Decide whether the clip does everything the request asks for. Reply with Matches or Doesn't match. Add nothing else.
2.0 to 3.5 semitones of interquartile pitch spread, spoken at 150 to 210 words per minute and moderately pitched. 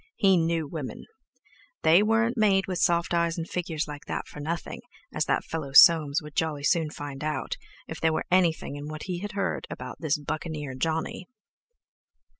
Matches